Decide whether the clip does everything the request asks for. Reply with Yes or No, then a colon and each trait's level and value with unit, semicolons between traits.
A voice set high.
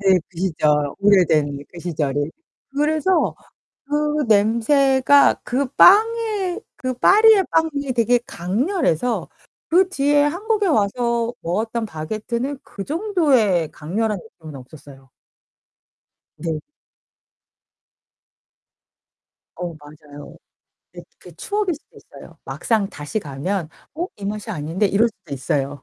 Yes: high, 220 Hz